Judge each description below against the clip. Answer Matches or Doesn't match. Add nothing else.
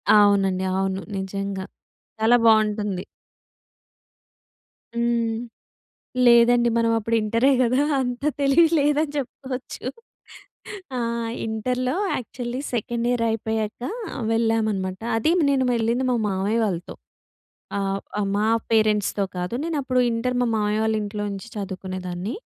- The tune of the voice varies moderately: Matches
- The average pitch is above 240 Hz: Doesn't match